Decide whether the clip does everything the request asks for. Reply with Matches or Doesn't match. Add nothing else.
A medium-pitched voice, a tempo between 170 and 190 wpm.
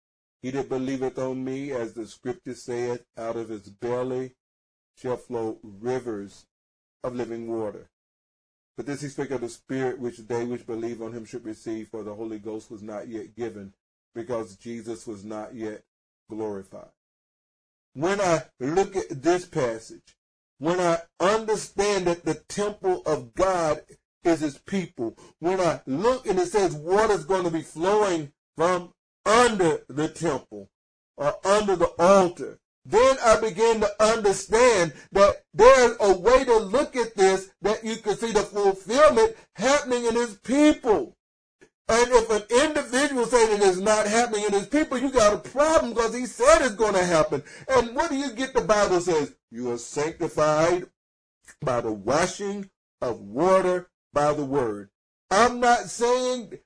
Doesn't match